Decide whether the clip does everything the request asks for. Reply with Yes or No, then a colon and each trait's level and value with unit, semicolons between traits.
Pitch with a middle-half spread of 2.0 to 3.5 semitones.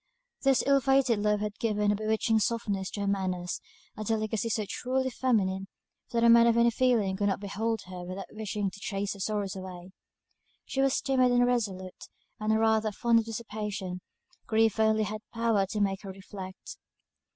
Yes: average, 2.8 semitones